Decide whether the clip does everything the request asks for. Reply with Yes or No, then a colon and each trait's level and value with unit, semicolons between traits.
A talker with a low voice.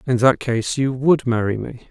Yes: low, 125 Hz